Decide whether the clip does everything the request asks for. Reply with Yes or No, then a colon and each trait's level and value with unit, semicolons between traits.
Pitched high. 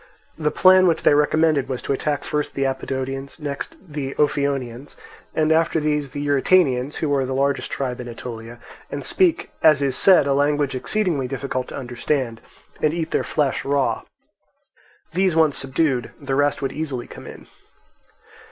No: medium, 140 Hz